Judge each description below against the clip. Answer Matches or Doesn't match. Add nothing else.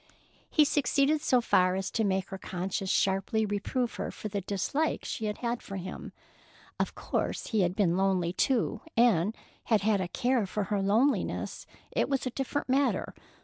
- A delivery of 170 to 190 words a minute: Matches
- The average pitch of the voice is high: Matches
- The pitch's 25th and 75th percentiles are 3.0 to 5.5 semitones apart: Matches